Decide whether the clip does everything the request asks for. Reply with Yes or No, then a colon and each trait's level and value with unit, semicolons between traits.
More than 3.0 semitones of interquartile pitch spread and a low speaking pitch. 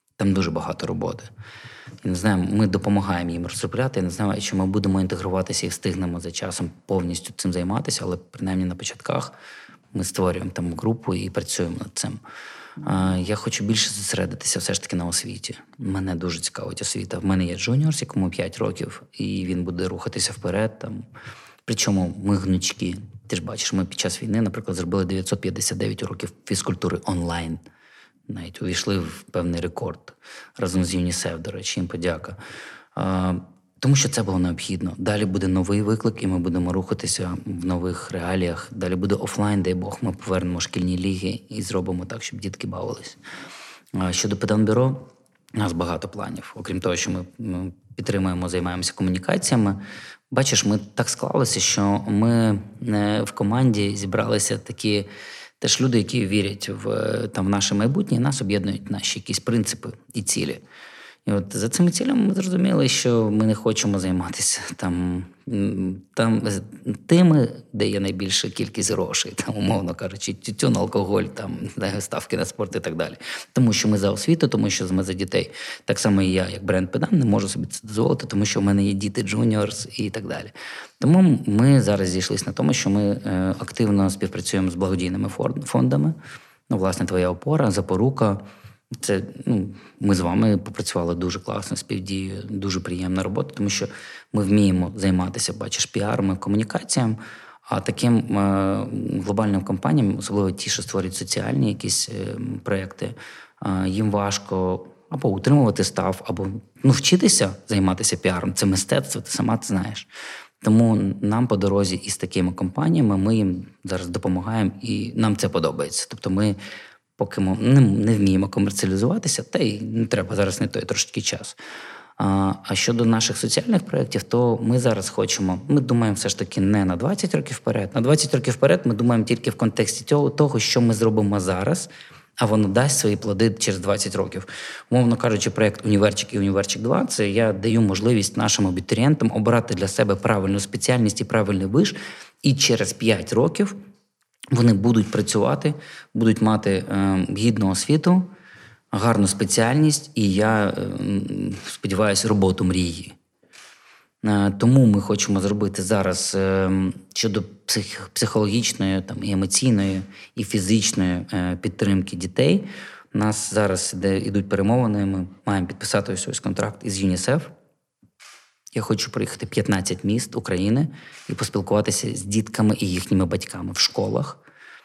Yes: average, 3.4 semitones; low, 100 Hz